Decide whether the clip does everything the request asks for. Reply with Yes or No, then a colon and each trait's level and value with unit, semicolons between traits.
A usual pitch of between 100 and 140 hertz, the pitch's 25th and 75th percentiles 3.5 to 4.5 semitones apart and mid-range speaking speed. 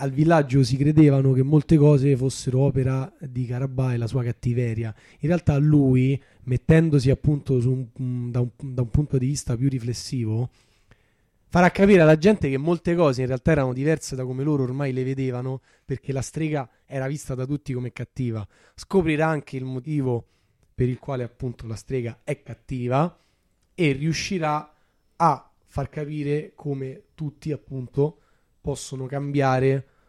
No: low, 135 Hz; average, 2.8 semitones; average, 160 wpm